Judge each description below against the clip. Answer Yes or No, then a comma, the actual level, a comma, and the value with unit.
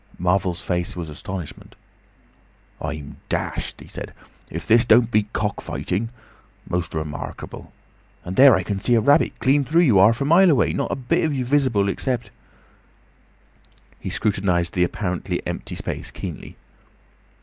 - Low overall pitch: Yes, low, 105 Hz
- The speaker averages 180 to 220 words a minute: No, average, 145 wpm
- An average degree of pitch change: No, wide, 6.4 semitones